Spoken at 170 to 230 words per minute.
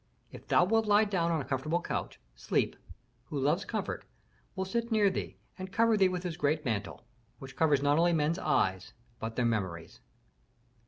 Yes: average, 180 wpm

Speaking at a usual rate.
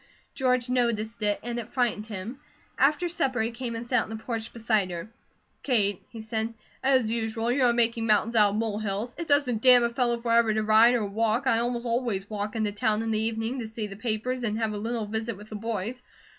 No: fast, 225 wpm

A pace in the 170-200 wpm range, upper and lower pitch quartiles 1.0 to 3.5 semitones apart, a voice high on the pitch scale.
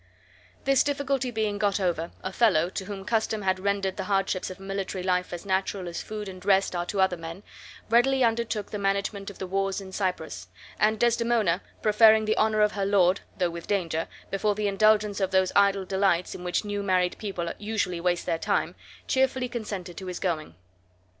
Yes: average, 190 wpm; average, 2.7 semitones; high, 195 Hz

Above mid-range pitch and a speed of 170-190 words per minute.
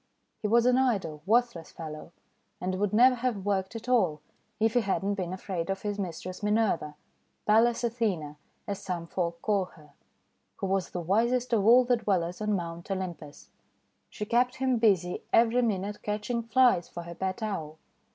Yes: high, 200 Hz; average, 180 wpm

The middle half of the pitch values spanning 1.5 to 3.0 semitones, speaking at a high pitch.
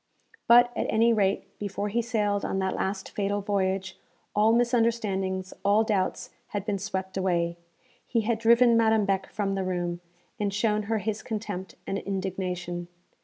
Yes: narrow, 2.6 semitones; high, 200 Hz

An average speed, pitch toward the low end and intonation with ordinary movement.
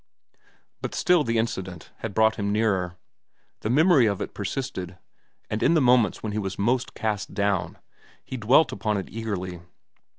Yes: average, 165 wpm; low, 110 Hz; average, 3.7 semitones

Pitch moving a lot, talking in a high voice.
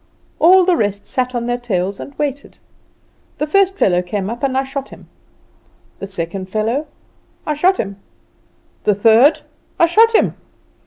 Yes: wide, 7.1 semitones; very high, 250 Hz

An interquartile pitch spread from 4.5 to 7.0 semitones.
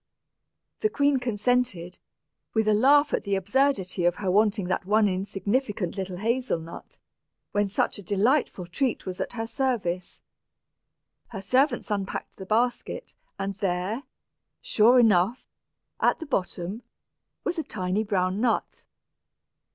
Yes: average, 4.8 semitones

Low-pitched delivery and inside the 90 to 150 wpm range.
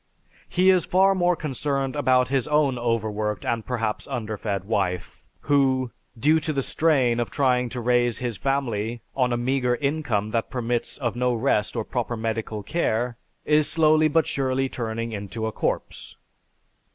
No: low, 125 Hz; average, 160 wpm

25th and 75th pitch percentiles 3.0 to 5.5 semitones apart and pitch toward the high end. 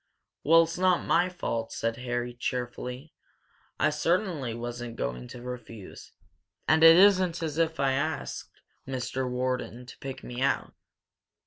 No: average, 5.1 semitones; low, 130 Hz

